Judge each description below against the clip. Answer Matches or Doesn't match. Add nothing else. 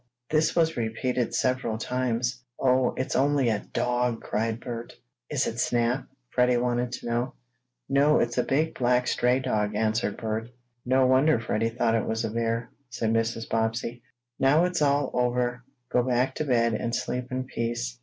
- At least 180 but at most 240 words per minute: Doesn't match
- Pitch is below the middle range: Matches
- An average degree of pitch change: Doesn't match